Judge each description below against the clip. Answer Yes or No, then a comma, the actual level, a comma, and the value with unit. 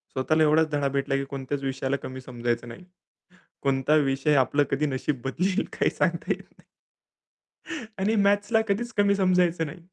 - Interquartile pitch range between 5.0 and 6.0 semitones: Yes, wide, 5.4 semitones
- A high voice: No, medium, 145 Hz